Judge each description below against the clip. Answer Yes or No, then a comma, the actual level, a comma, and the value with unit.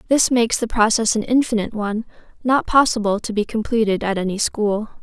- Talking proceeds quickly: No, average, 180 wpm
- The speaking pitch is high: Yes, high, 220 Hz